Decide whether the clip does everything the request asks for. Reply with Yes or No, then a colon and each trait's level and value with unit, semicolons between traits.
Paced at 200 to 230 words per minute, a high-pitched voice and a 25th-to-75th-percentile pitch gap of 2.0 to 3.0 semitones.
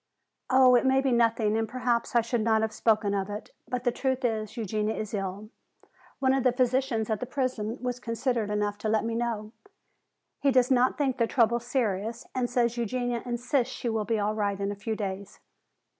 Yes: fast, 205 wpm; high, 230 Hz; average, 2.7 semitones